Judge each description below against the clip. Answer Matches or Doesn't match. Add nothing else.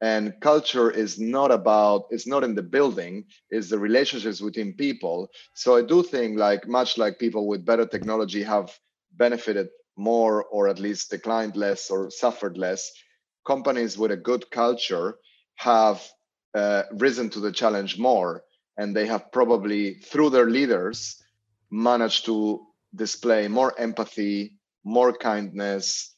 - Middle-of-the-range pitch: Doesn't match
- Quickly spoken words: Doesn't match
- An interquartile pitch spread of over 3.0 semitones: Doesn't match